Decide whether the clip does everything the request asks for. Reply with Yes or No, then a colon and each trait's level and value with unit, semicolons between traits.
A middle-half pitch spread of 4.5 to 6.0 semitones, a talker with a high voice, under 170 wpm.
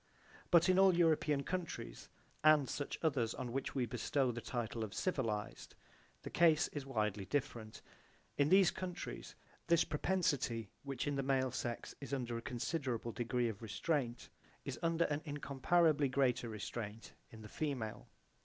No: average, 4.8 semitones; low, 135 Hz; average, 155 wpm